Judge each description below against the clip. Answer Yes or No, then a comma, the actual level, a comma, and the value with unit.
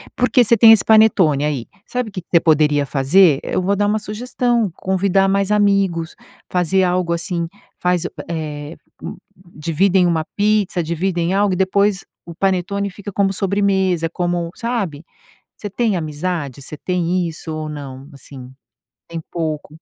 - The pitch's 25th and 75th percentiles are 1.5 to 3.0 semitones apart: No, average, 3.8 semitones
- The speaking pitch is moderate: Yes, medium, 180 Hz